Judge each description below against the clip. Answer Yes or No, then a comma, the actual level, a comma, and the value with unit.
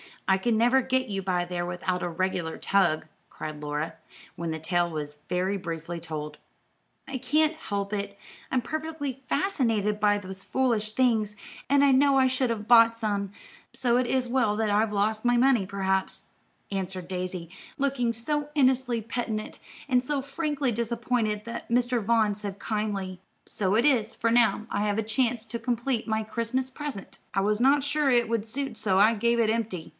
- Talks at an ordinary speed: Yes, average, 180 wpm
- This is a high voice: Yes, high, 220 Hz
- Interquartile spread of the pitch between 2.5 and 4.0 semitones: No, average, 4.5 semitones